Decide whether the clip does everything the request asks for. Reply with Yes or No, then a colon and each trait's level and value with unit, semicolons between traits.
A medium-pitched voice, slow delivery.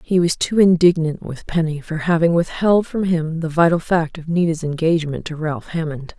No: medium, 165 Hz; average, 195 wpm